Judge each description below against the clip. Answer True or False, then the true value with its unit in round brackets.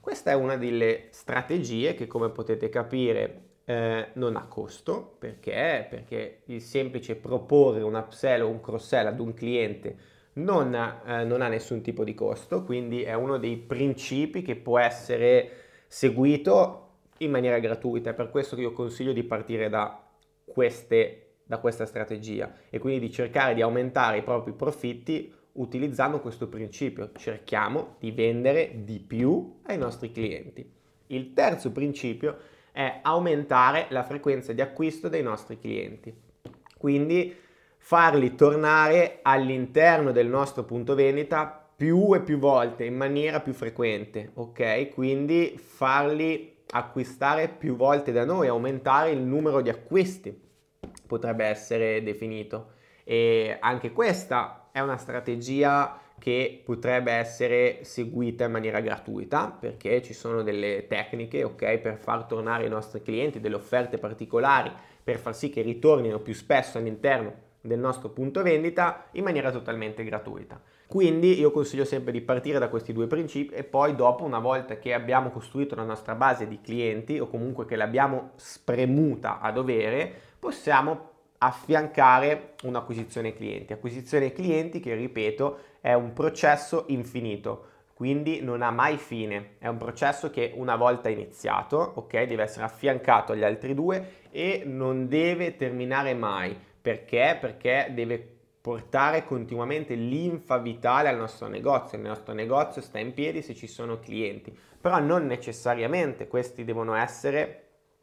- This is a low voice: True (125 Hz)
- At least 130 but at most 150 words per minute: True (145 wpm)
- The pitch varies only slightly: False (3.8 semitones)